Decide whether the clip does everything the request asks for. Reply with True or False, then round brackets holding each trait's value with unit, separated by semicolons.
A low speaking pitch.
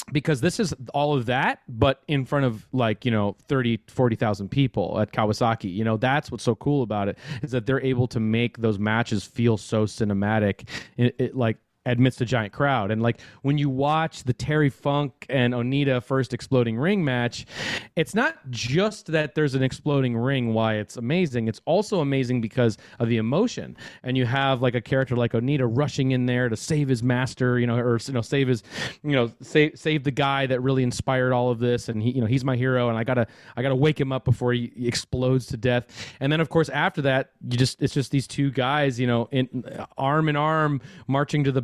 True (130 Hz)